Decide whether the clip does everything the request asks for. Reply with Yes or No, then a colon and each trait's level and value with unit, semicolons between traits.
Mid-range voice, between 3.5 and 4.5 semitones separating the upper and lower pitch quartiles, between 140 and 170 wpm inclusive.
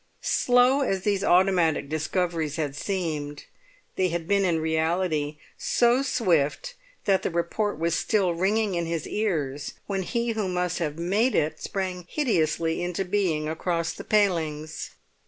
Yes: medium, 175 Hz; average, 4.0 semitones; average, 145 wpm